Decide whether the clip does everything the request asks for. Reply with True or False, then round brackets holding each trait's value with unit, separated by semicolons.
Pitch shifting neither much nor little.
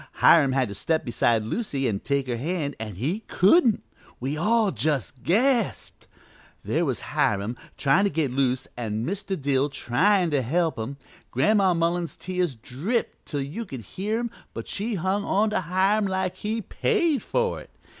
False (7.4 semitones)